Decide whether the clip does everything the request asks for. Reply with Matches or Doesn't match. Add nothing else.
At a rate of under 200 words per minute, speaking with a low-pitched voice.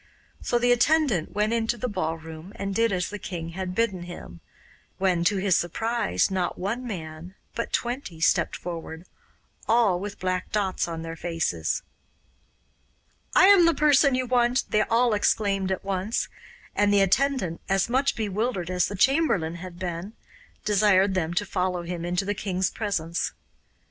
Doesn't match